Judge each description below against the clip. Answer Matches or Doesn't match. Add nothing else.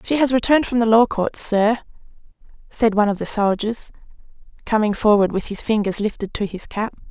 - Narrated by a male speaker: Doesn't match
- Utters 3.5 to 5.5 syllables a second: Doesn't match